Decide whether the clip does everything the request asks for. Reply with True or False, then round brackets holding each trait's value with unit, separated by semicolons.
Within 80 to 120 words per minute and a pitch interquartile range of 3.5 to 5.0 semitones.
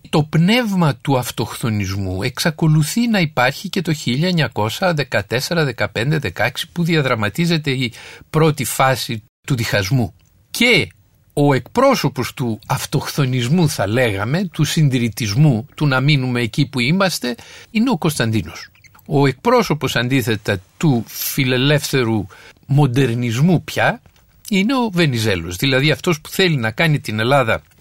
False (115 wpm; 5.5 semitones)